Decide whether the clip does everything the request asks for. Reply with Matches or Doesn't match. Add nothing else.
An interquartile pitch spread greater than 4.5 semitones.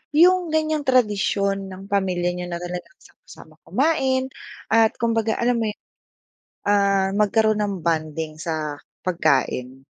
Matches